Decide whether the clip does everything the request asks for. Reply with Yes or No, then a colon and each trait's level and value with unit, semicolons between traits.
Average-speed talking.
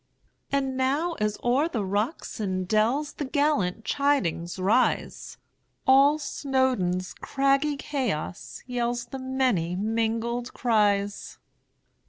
No: slow, 90 wpm